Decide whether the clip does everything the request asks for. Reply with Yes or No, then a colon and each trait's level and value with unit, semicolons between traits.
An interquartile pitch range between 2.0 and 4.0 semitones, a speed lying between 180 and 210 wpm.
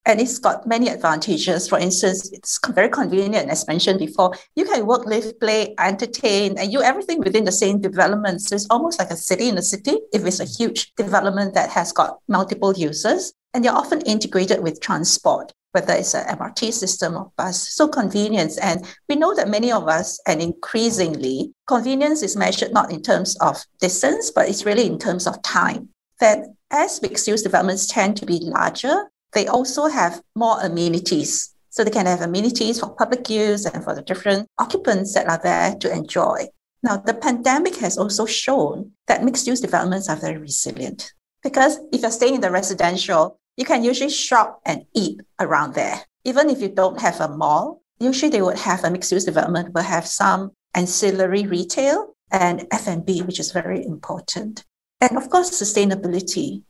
No: average, 5.2 semitones; average, 185 wpm